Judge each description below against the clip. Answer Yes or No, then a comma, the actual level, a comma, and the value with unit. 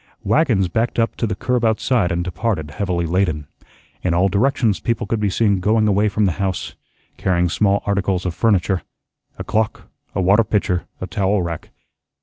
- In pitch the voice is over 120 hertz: No, low, 100 Hz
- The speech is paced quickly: No, average, 175 wpm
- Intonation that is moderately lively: Yes, average, 3.4 semitones